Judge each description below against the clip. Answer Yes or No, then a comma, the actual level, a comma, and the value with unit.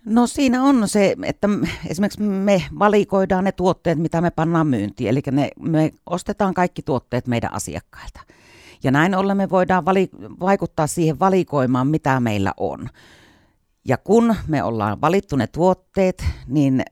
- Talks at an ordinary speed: Yes, average, 145 wpm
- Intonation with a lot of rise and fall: Yes, wide, 6.6 semitones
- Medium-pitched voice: Yes, medium, 165 Hz